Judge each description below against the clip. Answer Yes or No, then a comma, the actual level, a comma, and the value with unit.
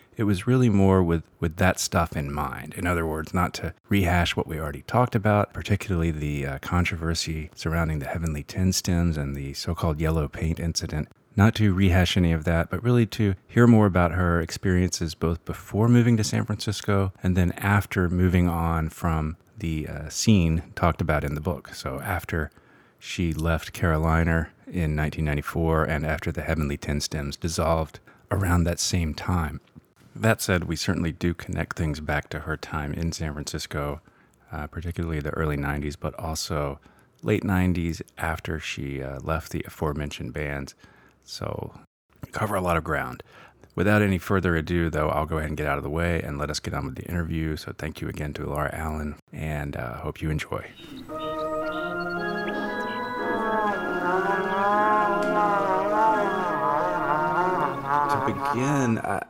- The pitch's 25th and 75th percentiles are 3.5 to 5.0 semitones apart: Yes, average, 4.3 semitones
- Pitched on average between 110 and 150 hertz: No, very low, 85 Hz